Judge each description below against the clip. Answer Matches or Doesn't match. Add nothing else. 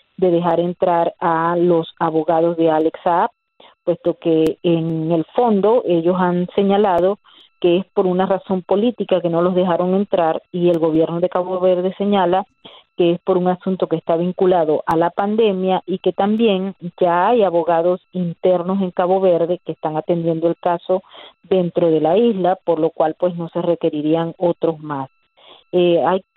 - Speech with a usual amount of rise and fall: Doesn't match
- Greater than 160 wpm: Matches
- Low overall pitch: Doesn't match